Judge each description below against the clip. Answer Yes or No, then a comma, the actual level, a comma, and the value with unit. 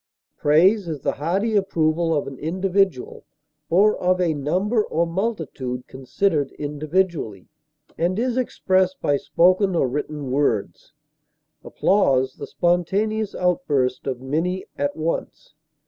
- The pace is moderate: No, slow, 120 wpm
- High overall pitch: No, medium, 170 Hz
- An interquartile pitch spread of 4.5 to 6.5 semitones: Yes, average, 4.8 semitones